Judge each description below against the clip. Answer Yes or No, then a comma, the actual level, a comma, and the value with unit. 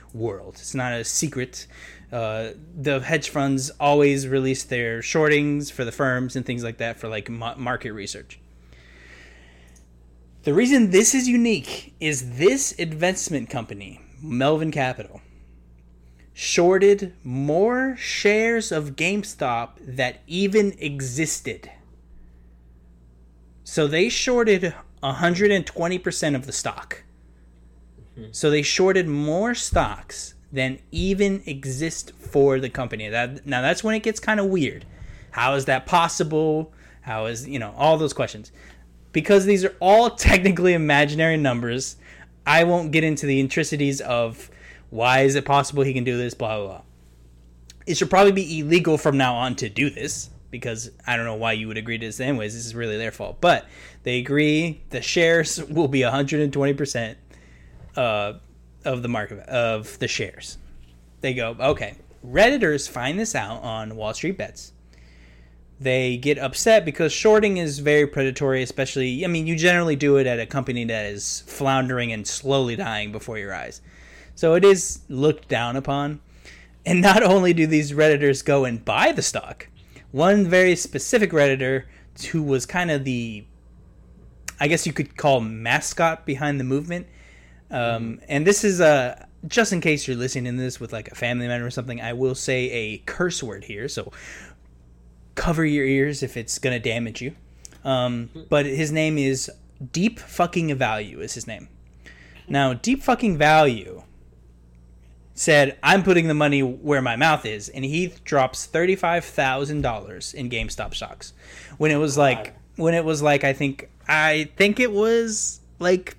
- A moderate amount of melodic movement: No, wide, 6.3 semitones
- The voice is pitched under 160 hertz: Yes, low, 135 Hz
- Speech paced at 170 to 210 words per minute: No, average, 160 wpm